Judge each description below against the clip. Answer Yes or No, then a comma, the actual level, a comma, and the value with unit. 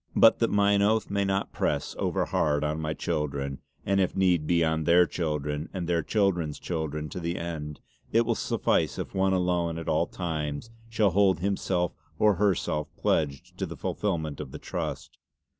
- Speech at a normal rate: Yes, average, 175 wpm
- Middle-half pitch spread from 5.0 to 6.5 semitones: No, average, 4.1 semitones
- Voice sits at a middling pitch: No, very low, 85 Hz